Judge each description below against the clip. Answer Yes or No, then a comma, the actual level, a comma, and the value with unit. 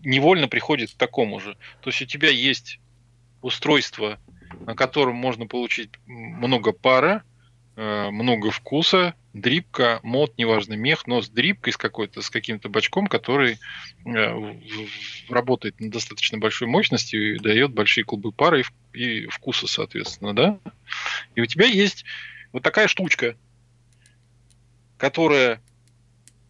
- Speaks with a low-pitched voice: Yes, low, 120 Hz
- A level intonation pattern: Yes, narrow, 2.0 semitones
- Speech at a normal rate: Yes, average, 130 wpm